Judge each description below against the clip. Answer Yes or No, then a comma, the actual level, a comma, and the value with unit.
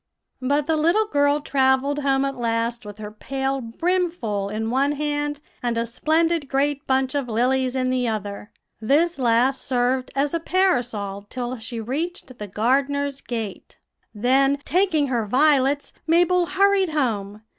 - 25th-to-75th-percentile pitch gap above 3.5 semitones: Yes, average, 4.0 semitones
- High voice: Yes, very high, 265 Hz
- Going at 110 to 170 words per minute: Yes, average, 150 wpm